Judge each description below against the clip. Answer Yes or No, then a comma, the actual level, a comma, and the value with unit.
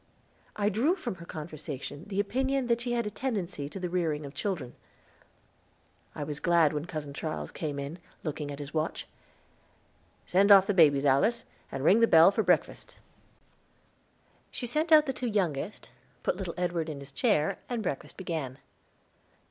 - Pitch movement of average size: No, wide, 6.2 semitones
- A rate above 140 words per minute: Yes, average, 170 wpm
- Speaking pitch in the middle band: Yes, medium, 175 Hz